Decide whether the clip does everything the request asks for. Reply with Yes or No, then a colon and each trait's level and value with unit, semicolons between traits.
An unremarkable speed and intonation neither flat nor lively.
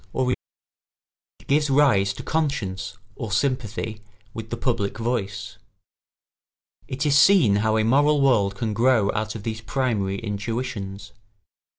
No: slow, 130 wpm; average, 4.3 semitones